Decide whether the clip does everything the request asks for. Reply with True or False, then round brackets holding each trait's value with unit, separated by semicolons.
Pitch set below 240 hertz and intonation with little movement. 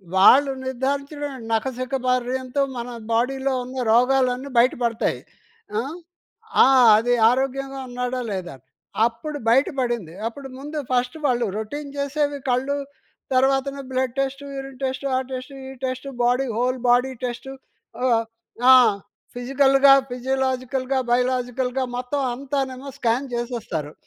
False (255 Hz; 1.7 semitones)